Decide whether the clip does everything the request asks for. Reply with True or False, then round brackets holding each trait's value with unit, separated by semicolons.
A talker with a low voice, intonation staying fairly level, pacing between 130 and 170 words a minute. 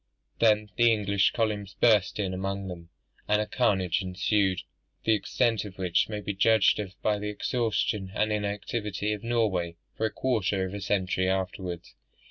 True (100 Hz; 2.3 semitones; 165 wpm)